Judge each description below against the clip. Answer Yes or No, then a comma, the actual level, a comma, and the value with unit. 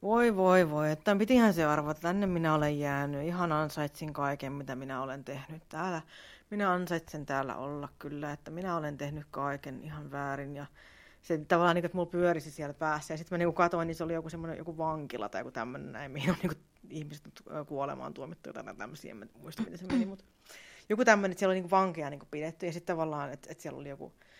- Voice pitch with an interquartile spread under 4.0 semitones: Yes, average, 3.2 semitones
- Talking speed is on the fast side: Yes, fast, 210 wpm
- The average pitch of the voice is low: No, medium, 160 Hz